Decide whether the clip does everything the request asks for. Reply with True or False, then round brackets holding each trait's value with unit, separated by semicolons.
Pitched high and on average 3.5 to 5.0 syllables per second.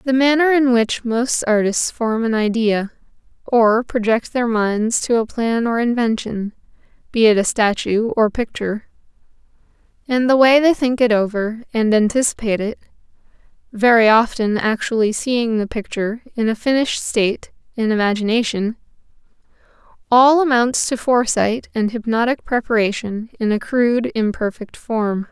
True (230 Hz; 4.8 syllables/s)